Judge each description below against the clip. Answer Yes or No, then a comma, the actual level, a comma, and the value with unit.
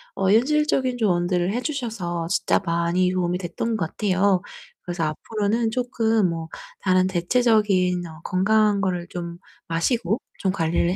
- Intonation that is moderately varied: Yes, average, 4.2 semitones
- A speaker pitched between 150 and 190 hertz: Yes, medium, 185 Hz